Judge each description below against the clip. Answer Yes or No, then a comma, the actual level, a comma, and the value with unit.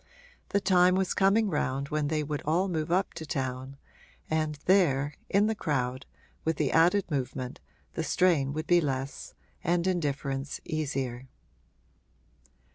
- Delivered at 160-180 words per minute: No, average, 140 wpm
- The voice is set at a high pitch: No, medium, 155 Hz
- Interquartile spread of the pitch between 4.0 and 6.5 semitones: Yes, average, 4.6 semitones